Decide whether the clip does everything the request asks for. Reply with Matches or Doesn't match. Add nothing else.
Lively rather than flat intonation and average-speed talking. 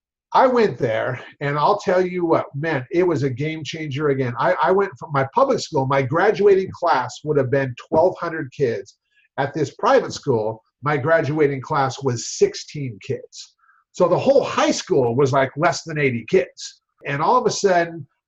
Matches